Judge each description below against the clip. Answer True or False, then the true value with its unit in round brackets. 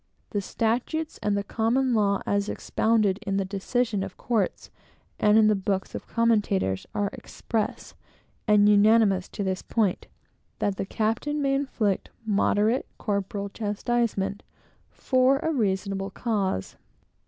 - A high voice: True (210 Hz)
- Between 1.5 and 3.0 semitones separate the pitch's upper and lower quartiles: True (2.7 semitones)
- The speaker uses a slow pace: True (130 wpm)